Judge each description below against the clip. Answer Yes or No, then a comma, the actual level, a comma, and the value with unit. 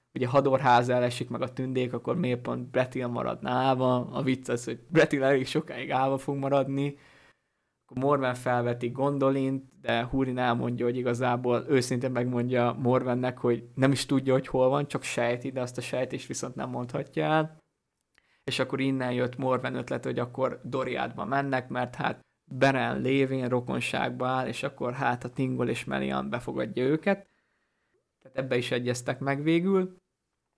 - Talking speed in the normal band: No, fast, 160 wpm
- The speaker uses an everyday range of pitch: No, narrow, 1.8 semitones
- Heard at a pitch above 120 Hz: Yes, low, 130 Hz